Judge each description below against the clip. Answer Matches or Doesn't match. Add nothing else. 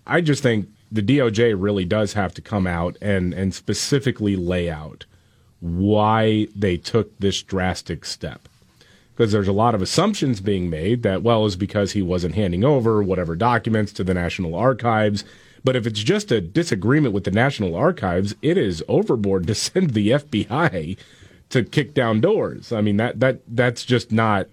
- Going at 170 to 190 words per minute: Matches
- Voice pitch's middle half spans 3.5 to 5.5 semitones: Matches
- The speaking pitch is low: Matches